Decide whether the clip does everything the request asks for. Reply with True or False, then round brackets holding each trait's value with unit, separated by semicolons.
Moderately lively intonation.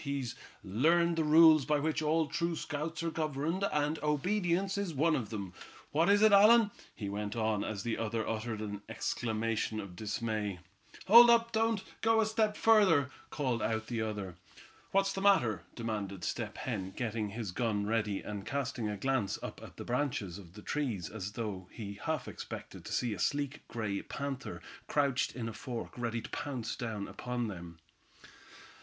False (7.0 semitones)